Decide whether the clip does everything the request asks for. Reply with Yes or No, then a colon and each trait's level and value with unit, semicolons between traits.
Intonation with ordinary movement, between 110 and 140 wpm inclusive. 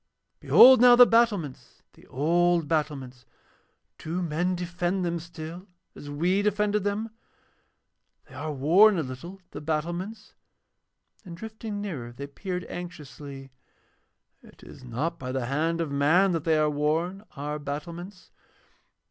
Yes: average, 4.3 semitones; slow, 135 wpm